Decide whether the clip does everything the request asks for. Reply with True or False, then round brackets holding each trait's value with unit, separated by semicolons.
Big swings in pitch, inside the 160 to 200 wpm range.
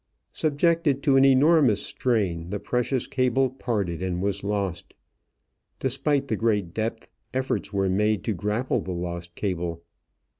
False (6.0 semitones; 140 wpm)